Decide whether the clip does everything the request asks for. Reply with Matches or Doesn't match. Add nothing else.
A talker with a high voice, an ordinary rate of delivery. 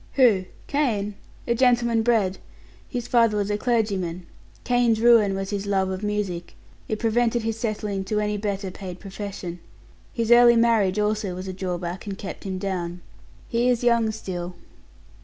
Matches